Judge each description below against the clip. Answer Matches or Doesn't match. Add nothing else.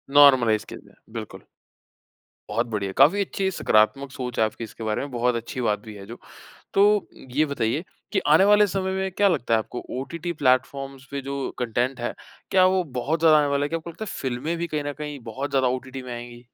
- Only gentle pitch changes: Doesn't match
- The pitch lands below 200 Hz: Matches